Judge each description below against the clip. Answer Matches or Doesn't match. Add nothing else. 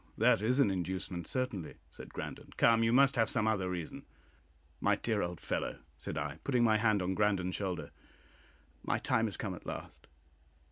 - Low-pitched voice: Matches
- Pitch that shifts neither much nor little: Matches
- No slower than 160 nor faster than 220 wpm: Matches